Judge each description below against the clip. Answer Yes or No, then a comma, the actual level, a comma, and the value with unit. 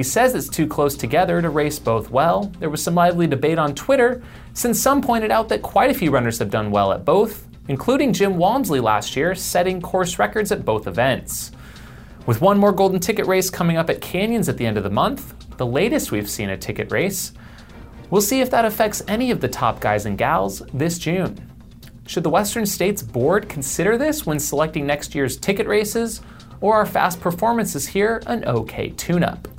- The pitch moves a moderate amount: No, wide, 7.2 semitones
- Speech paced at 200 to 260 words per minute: Yes, fast, 205 wpm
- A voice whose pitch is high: No, medium, 180 Hz